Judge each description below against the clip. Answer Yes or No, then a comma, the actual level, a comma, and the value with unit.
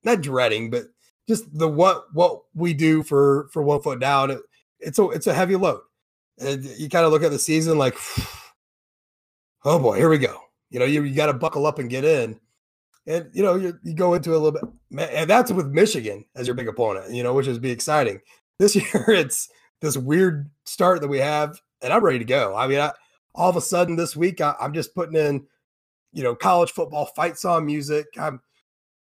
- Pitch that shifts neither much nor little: Yes, average, 3.8 semitones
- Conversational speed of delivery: No, fast, 220 wpm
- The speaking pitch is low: No, medium, 155 Hz